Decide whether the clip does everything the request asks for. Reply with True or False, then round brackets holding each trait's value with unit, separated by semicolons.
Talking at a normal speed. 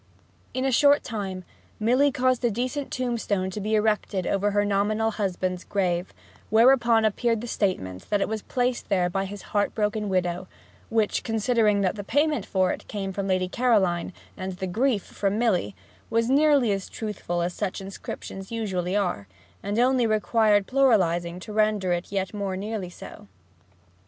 True (160 wpm)